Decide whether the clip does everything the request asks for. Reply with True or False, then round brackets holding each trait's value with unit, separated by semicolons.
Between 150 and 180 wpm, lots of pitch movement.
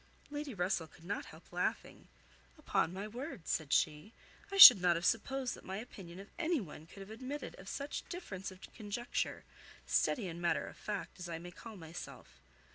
False (190 wpm; 5.8 semitones)